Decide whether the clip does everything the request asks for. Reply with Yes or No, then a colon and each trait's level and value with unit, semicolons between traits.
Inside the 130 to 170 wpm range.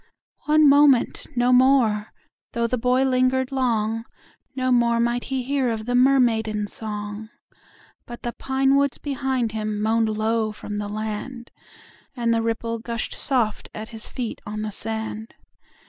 Yes: average, 140 wpm